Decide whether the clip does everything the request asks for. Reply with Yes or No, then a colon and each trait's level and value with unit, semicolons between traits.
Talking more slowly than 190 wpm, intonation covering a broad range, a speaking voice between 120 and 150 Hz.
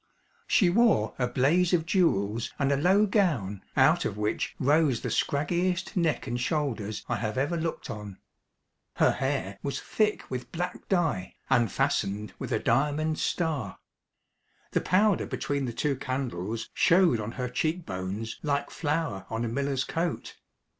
Yes: average, 155 wpm; wide, 6.9 semitones; medium, 140 Hz